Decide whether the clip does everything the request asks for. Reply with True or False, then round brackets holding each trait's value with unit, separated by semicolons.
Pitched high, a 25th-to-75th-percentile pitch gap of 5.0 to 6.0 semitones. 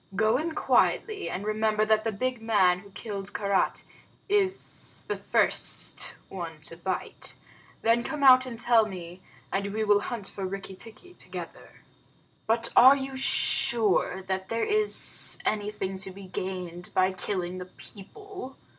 False (210 Hz; 4.0 semitones)